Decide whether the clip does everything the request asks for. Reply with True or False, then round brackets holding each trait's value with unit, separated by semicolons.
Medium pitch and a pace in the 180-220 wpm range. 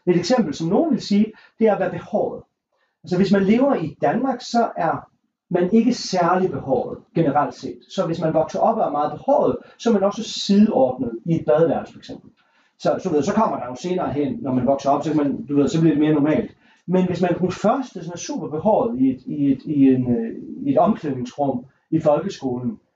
True (180 Hz; 215 wpm)